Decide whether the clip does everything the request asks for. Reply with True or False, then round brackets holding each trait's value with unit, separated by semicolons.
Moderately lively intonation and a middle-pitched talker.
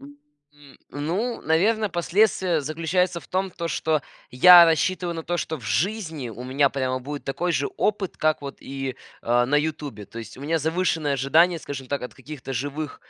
True (4.0 semitones; 150 Hz)